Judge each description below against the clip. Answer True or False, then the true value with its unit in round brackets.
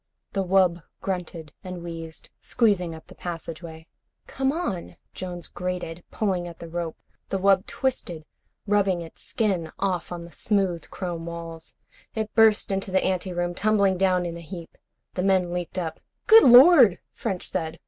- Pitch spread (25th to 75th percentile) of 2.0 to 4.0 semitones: True (2.6 semitones)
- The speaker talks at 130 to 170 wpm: True (160 wpm)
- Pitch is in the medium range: True (180 Hz)